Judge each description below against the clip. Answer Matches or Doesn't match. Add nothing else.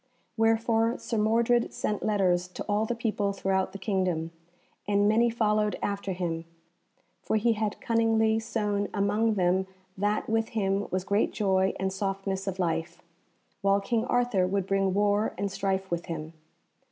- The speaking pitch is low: Doesn't match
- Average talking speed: Matches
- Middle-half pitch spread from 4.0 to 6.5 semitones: Doesn't match